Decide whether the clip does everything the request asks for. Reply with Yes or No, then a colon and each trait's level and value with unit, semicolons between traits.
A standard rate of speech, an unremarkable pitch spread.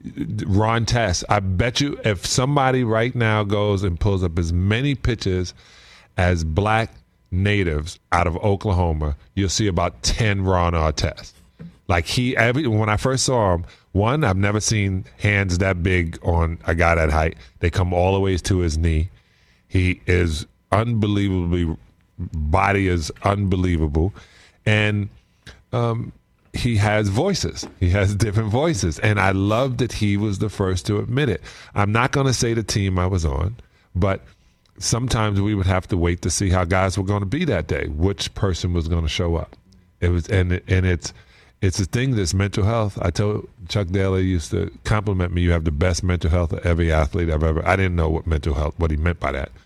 Yes: average, 190 wpm; average, 3.4 semitones